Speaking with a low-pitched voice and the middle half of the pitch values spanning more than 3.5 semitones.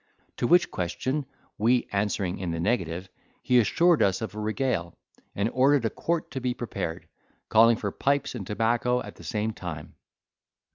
Yes: low, 110 Hz; average, 4.7 semitones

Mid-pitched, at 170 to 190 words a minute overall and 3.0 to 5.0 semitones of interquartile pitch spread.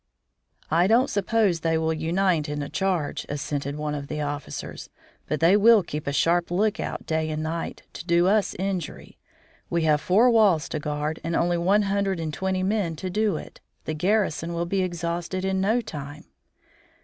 Yes: medium, 170 Hz; average, 185 wpm; average, 3.8 semitones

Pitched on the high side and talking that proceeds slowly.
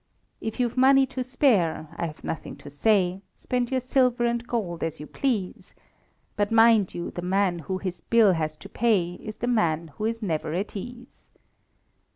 No: high, 205 Hz; average, 185 wpm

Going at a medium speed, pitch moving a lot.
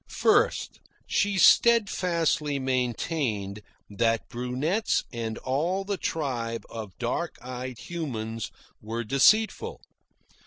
No: slow, 90 wpm; wide, 6.7 semitones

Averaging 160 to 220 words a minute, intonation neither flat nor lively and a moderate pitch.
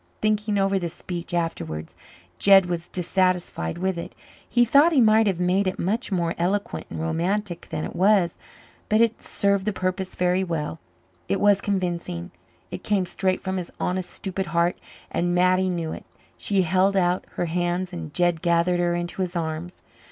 No: average, 175 wpm; narrow, 2.2 semitones; medium, 180 Hz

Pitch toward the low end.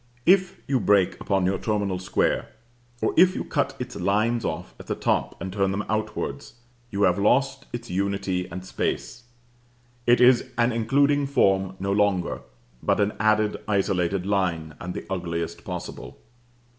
Yes: low, 100 Hz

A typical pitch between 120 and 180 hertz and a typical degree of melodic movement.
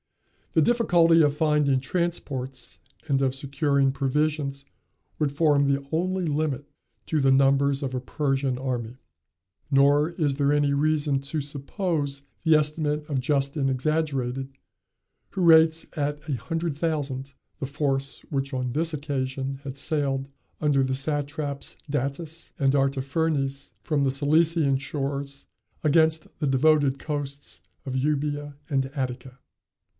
No: medium, 140 Hz; narrow, 2.2 semitones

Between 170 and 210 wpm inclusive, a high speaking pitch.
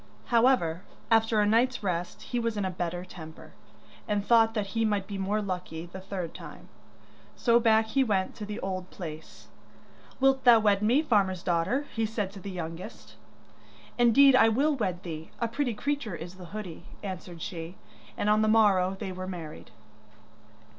Yes: average, 175 wpm; high, 205 Hz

